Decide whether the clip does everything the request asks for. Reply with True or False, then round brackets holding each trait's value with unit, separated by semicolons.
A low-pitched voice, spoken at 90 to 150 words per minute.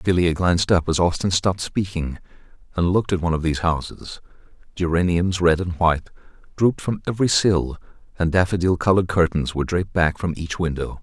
False (85 Hz; 175 wpm)